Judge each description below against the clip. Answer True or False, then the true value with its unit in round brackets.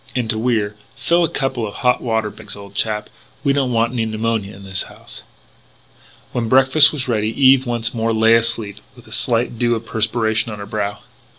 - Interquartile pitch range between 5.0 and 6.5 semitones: False (2.4 semitones)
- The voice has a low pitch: True (115 Hz)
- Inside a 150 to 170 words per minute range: False (200 wpm)